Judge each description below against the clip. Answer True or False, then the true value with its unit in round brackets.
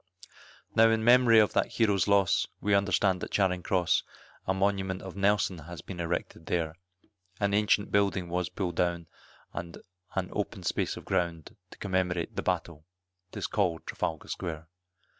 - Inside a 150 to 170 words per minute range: True (160 wpm)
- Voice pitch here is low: True (95 Hz)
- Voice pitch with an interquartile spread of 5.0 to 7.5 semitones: False (2.7 semitones)